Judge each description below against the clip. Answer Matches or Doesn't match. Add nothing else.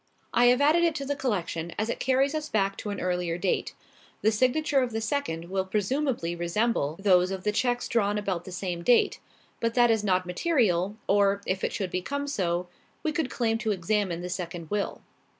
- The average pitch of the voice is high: Matches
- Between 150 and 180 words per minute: Doesn't match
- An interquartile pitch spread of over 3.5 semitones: Matches